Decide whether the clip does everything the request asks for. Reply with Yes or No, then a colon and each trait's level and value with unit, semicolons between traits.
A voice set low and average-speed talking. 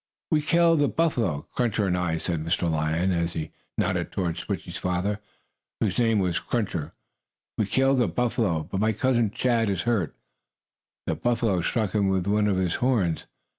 Yes: low, 100 Hz; average, 170 wpm